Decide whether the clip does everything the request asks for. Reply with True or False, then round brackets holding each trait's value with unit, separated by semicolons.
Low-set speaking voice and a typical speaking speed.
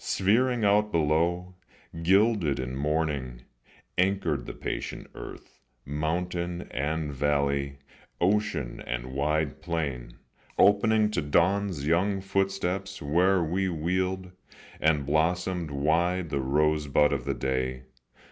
False (80 Hz; 110 wpm)